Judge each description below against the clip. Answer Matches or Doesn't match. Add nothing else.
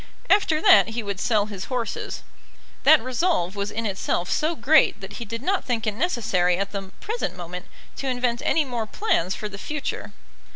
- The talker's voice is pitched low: Doesn't match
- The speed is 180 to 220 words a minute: Matches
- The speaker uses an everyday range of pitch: Doesn't match